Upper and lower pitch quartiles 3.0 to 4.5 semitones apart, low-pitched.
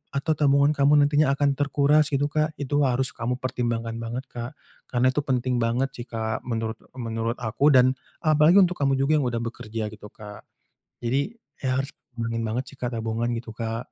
Yes: average, 3.6 semitones; low, 125 Hz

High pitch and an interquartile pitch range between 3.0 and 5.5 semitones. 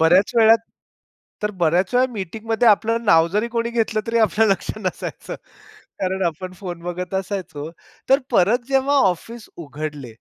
Yes: high, 195 Hz; average, 4.5 semitones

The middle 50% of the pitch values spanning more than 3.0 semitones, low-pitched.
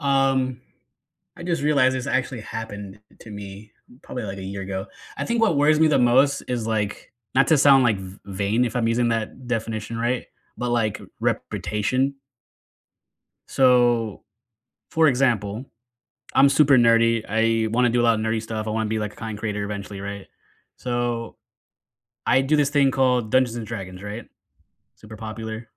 Yes: average, 3.4 semitones; low, 115 Hz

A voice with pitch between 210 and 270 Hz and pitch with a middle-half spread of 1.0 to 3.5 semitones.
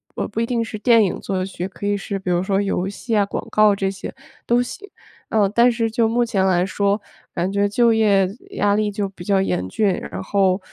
No: high, 200 Hz; narrow, 2.6 semitones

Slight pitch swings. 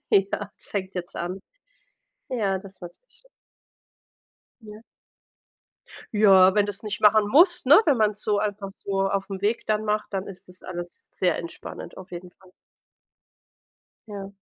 Yes: narrow, 2.0 semitones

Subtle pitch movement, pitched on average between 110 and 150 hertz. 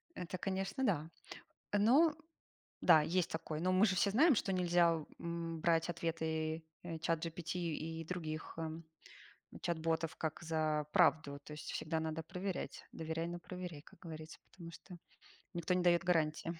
No: narrow, 2.1 semitones; medium, 165 Hz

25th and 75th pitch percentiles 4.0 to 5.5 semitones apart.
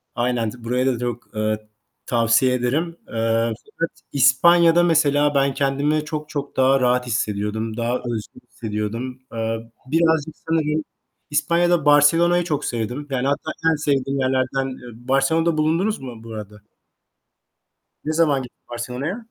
Yes: average, 4.4 semitones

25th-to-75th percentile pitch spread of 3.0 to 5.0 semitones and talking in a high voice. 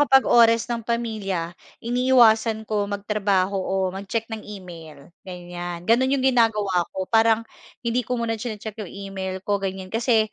Yes: average, 3.5 semitones; high, 215 Hz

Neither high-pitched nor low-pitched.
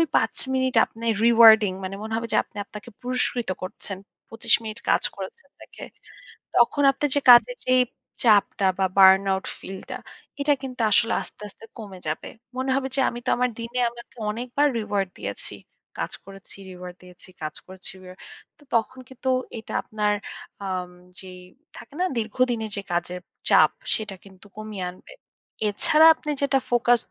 No: high, 220 Hz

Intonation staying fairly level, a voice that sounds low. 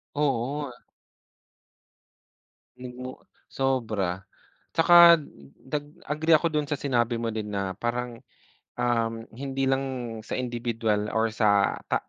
No: average, 3.3 semitones; low, 125 Hz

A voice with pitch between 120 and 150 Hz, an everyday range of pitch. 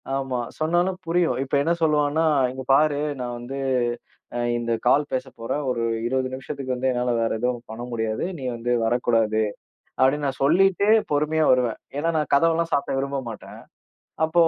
Yes: low, 135 Hz; average, 3.9 semitones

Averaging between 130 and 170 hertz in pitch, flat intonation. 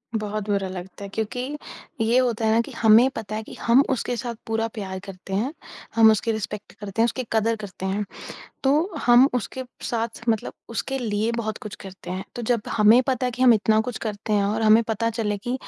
No: high, 220 Hz; narrow, 2.3 semitones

